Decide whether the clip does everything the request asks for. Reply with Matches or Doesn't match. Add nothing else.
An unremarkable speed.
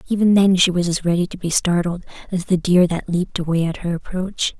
Doesn't match